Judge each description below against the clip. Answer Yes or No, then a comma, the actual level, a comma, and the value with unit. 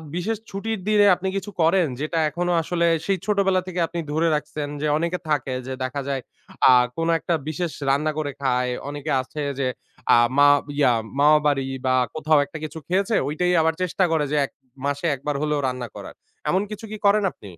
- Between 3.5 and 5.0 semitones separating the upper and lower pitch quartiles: Yes, average, 4.1 semitones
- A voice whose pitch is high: No, medium, 155 Hz